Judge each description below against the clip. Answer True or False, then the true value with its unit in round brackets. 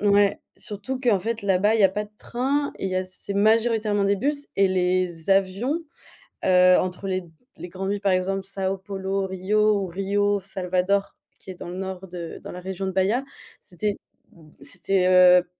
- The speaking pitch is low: False (195 Hz)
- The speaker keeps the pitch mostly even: True (1.9 semitones)